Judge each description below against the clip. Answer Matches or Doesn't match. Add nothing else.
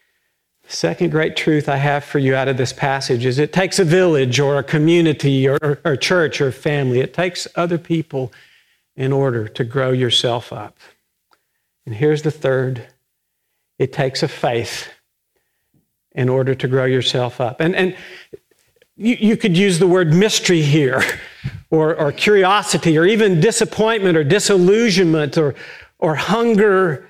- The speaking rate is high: Doesn't match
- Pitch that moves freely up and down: Matches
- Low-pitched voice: Doesn't match